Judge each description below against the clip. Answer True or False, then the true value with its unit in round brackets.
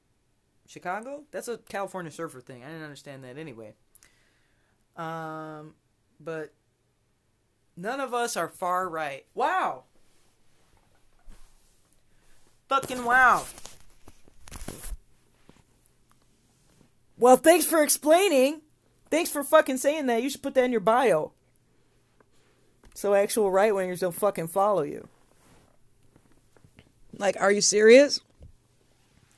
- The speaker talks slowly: True (100 wpm)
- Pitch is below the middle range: False (185 Hz)